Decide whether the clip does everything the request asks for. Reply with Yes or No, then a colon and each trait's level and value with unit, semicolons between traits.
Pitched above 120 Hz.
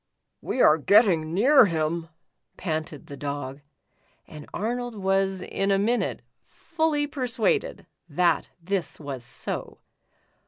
Yes: high, 190 Hz